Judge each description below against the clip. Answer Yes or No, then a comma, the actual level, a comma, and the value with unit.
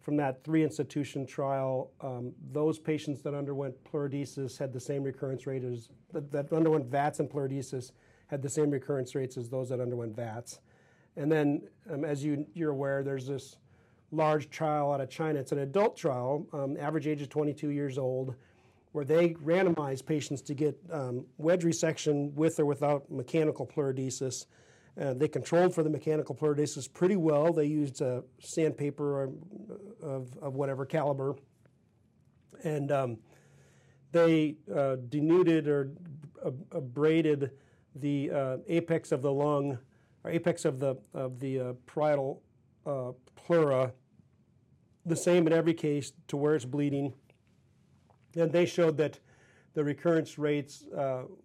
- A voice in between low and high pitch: Yes, medium, 145 Hz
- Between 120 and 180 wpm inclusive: Yes, average, 155 wpm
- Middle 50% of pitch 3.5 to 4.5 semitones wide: No, narrow, 2.6 semitones